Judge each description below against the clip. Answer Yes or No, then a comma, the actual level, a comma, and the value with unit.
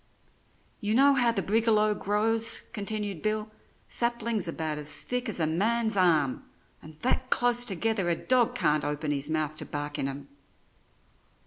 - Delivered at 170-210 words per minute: No, average, 155 wpm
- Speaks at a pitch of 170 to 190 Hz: No, high, 210 Hz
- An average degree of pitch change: No, wide, 6.8 semitones